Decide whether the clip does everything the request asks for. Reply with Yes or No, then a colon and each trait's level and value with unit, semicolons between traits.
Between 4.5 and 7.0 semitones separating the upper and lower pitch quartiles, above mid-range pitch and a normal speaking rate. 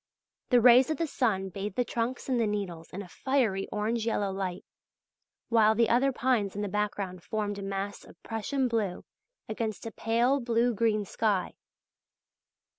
No: average, 3.1 semitones; high, 220 Hz; average, 170 wpm